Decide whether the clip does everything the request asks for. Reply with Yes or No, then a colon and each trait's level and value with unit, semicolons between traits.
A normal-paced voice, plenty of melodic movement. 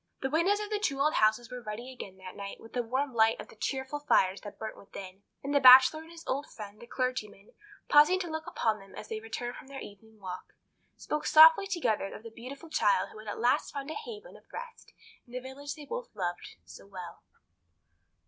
No: fast, 225 wpm; wide, 5.9 semitones